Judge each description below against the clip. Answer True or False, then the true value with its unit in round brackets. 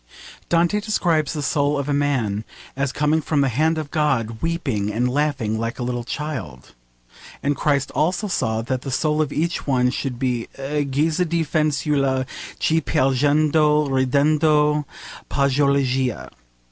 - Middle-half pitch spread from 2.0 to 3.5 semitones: True (2.9 semitones)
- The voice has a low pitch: False (145 Hz)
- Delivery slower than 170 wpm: True (150 wpm)